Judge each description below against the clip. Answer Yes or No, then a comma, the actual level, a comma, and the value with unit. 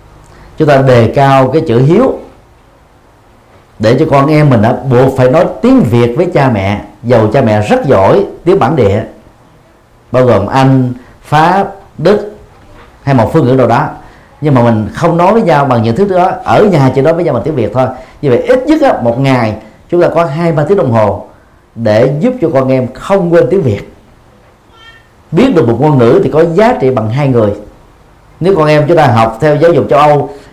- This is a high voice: No, low, 130 Hz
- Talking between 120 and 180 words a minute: No, average, 210 wpm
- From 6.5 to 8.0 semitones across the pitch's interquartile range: No, wide, 5.5 semitones